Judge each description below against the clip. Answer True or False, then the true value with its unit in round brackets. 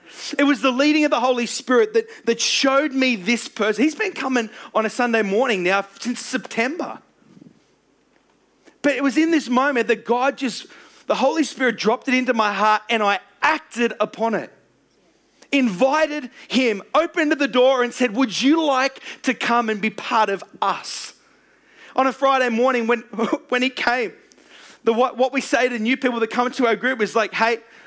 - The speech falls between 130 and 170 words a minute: False (185 wpm)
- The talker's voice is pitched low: False (250 Hz)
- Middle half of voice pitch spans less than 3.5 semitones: True (3.0 semitones)